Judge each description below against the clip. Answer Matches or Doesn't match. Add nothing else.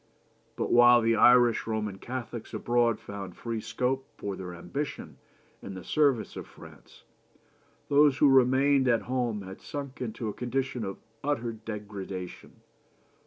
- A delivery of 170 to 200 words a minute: Doesn't match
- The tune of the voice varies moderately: Matches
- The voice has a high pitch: Doesn't match